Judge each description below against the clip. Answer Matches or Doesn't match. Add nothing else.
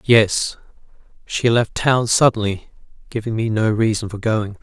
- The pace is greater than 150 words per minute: Doesn't match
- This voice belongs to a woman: Doesn't match